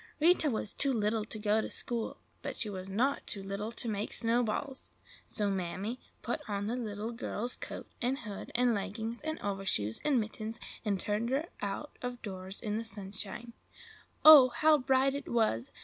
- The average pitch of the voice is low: No, high, 220 Hz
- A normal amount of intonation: Yes, average, 3.5 semitones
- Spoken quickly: No, average, 180 wpm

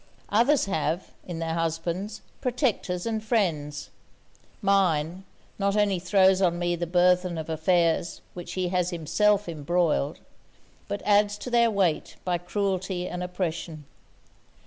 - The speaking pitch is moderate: Yes, medium, 180 Hz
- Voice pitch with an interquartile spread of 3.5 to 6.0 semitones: No, average, 3.1 semitones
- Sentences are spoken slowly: Yes, slow, 130 wpm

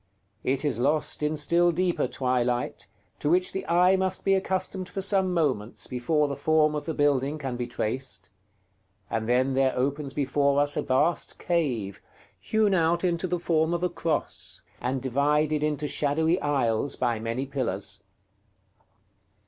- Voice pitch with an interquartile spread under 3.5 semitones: No, average, 4.6 semitones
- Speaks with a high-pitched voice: No, medium, 145 Hz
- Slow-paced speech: No, average, 155 wpm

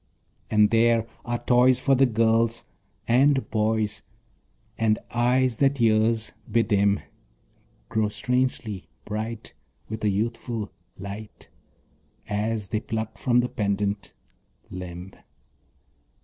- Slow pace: Yes, slow, 105 wpm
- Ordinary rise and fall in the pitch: No, narrow, 2.2 semitones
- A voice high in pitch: No, low, 110 Hz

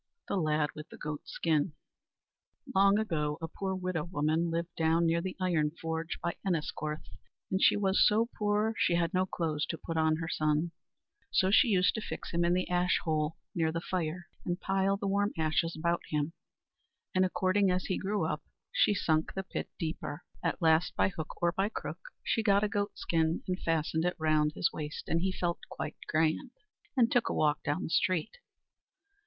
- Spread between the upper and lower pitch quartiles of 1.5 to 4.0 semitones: Yes, average, 3.2 semitones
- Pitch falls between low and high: Yes, medium, 170 Hz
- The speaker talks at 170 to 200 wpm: Yes, average, 195 wpm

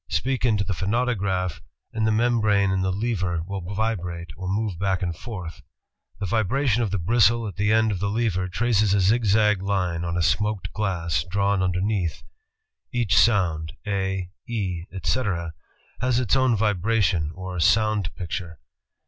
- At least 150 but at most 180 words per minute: Yes, average, 155 wpm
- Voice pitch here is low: Yes, low, 100 Hz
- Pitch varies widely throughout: No, average, 3.3 semitones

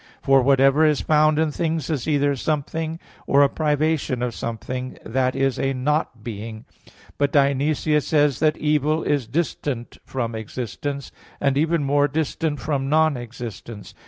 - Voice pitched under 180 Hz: Yes, medium, 140 Hz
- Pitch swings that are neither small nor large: Yes, average, 3.0 semitones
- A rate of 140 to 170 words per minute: Yes, average, 160 wpm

